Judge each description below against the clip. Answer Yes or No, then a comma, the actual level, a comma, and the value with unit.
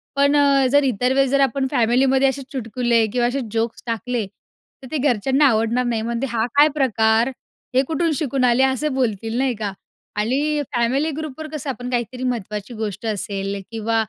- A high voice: Yes, very high, 250 Hz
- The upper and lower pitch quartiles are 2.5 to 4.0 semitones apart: Yes, average, 3.2 semitones